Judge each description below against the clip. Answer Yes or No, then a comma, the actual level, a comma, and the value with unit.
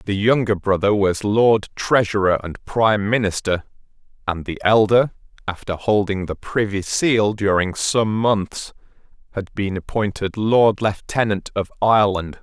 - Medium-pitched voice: No, low, 105 Hz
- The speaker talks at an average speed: No, slow, 130 wpm